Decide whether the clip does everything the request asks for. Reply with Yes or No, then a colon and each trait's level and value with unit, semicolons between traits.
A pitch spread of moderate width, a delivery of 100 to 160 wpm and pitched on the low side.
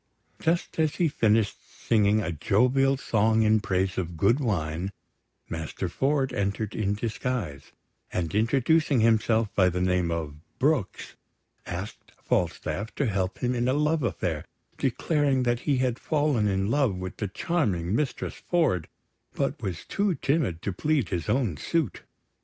No: wide, 6.6 semitones; average, 150 wpm; low, 110 Hz